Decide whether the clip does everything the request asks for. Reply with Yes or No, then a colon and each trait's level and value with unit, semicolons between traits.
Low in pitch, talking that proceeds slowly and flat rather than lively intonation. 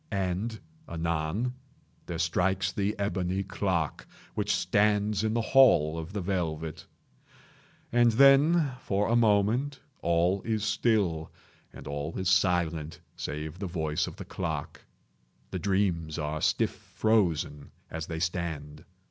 No: very low, 95 Hz; slow, 130 wpm; average, 4.5 semitones